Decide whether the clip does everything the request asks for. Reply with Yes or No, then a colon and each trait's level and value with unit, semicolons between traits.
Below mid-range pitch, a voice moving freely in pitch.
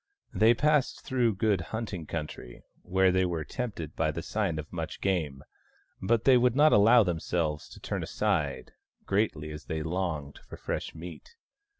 Yes: very low, 90 Hz; wide, 6.0 semitones